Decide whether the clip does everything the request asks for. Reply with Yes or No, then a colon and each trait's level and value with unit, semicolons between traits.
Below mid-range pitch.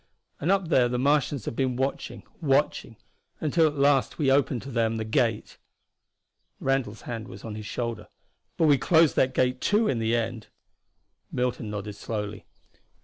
Yes: low, 125 Hz